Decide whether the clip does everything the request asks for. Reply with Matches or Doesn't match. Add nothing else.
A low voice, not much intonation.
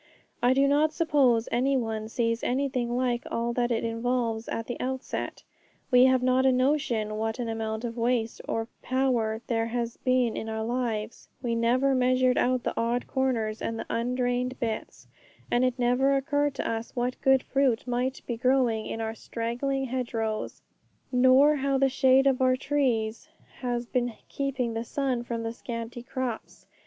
Doesn't match